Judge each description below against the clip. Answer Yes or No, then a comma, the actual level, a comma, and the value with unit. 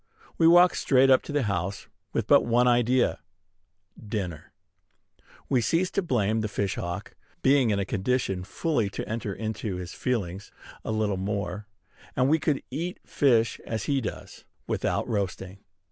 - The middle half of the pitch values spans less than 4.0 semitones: No, average, 4.8 semitones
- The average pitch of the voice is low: Yes, low, 110 Hz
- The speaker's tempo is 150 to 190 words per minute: Yes, average, 160 wpm